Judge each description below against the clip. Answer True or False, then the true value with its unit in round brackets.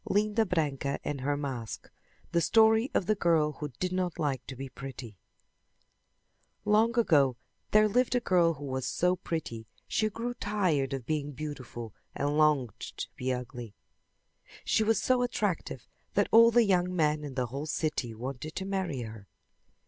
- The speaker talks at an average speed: True (165 wpm)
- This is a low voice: False (155 Hz)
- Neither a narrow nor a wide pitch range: False (7.2 semitones)